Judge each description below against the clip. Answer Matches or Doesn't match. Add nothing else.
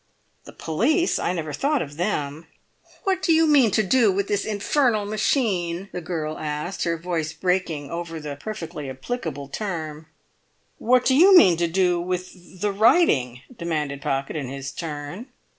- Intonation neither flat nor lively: Doesn't match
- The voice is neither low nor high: Matches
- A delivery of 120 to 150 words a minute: Doesn't match